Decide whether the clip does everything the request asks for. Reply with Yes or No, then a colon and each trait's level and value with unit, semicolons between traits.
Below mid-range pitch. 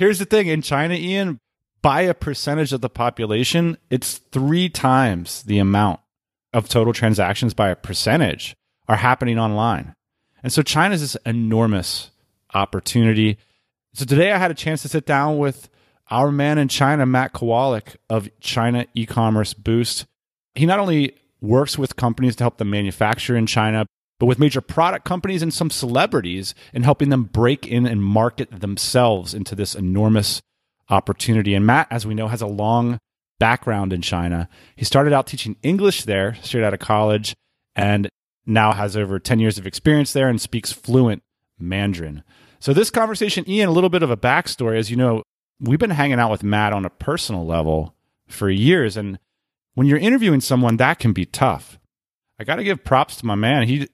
Yes: low, 120 Hz